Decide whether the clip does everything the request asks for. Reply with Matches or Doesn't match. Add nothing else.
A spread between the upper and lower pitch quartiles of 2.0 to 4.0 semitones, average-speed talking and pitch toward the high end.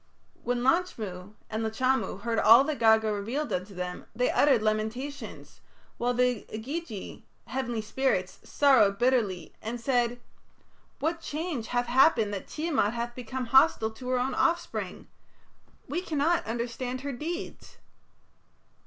Doesn't match